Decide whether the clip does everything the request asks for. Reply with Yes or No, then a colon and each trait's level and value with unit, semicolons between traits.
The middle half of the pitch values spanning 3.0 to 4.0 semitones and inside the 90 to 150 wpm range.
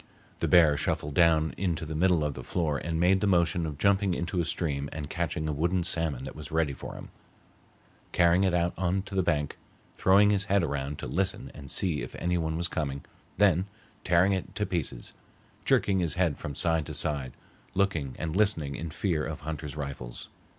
No: average, 3.5 semitones; average, 200 wpm